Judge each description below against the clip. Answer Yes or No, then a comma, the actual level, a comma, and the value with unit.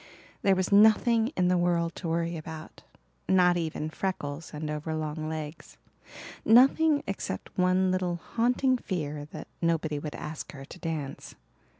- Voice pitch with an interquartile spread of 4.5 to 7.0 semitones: No, average, 3.3 semitones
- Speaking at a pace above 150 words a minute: No, average, 145 wpm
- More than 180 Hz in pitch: No, medium, 170 Hz